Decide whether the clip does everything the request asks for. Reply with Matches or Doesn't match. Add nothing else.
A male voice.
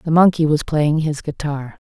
Doesn't match